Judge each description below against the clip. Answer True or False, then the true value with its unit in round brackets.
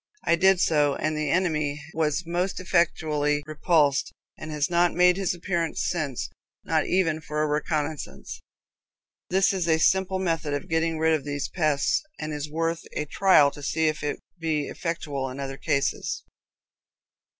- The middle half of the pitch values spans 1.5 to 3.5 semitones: True (2.6 semitones)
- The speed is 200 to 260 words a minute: False (160 wpm)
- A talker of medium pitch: True (155 Hz)